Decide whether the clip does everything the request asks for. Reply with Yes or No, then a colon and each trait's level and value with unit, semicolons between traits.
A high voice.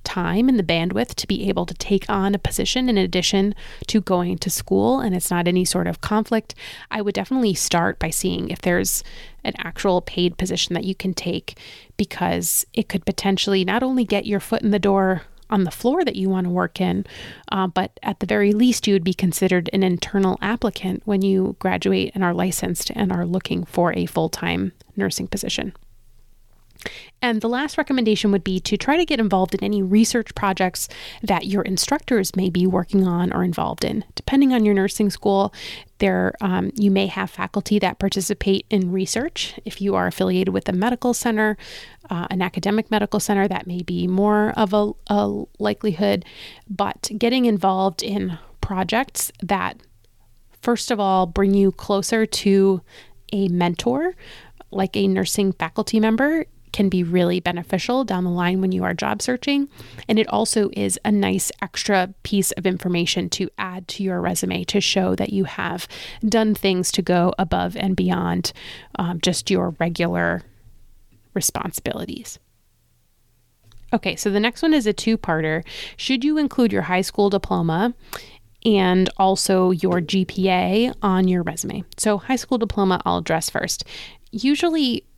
Yes: high, 195 Hz